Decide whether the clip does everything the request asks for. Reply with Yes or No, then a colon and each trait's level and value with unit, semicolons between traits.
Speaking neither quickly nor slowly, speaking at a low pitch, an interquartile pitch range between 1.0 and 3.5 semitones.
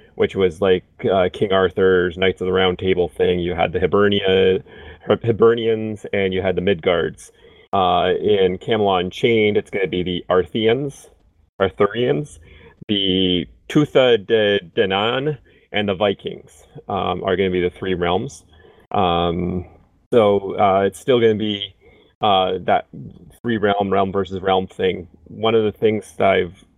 Yes: average, 155 wpm; very low, 95 Hz; average, 3.0 semitones